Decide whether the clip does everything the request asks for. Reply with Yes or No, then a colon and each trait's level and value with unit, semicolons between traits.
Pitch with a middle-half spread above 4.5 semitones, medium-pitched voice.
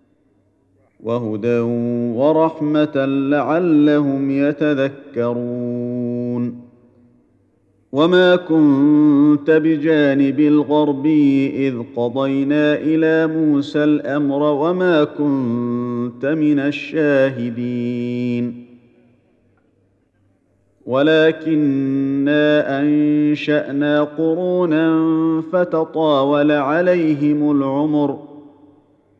No: average, 3.7 semitones; medium, 145 Hz